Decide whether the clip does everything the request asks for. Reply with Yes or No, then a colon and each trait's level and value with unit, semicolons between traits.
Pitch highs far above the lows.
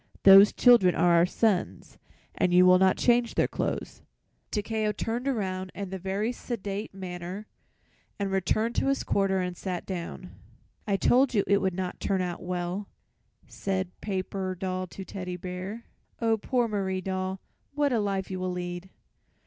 No: narrow, 2.4 semitones